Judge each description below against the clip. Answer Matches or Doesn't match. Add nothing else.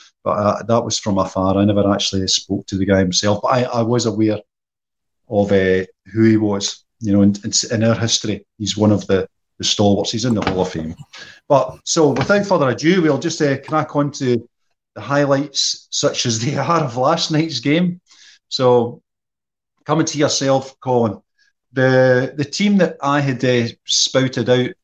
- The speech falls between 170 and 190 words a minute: Matches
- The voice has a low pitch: Matches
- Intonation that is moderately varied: Doesn't match